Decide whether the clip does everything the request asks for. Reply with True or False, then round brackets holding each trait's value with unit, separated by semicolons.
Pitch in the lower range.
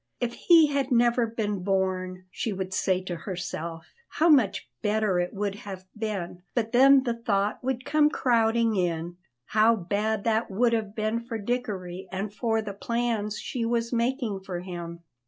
False (215 Hz)